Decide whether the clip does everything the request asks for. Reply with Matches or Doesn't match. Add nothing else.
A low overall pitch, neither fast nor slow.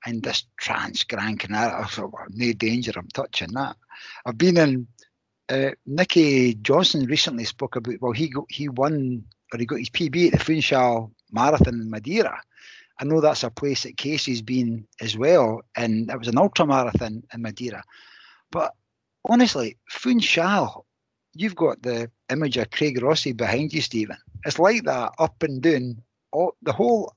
Matches